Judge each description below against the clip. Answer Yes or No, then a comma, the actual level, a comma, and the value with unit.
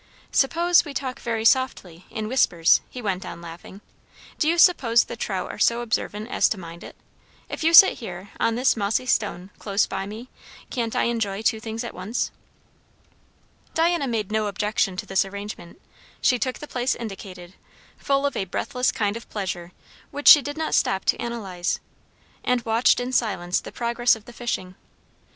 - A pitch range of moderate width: Yes, average, 4.5 semitones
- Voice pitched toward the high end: Yes, high, 225 Hz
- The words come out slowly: No, average, 180 wpm